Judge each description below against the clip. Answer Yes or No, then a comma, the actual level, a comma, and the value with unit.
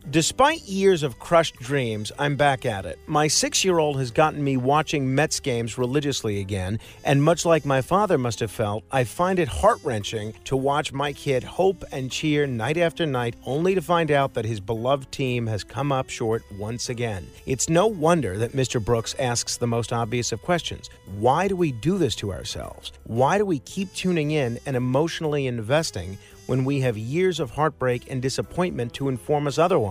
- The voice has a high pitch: No, low, 135 Hz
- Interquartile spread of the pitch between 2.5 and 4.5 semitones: No, average, 4.9 semitones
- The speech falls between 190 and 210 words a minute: Yes, average, 195 wpm